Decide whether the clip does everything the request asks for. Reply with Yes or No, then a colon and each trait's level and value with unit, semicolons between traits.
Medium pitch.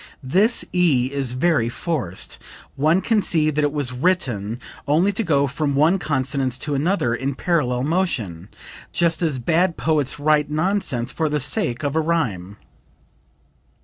Yes: medium, 145 Hz